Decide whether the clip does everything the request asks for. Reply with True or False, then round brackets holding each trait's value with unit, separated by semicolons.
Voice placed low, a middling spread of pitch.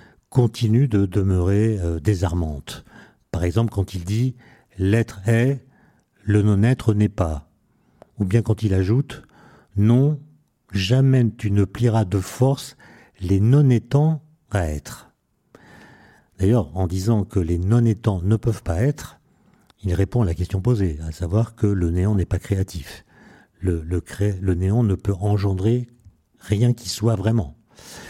True (105 Hz; 3.8 semitones)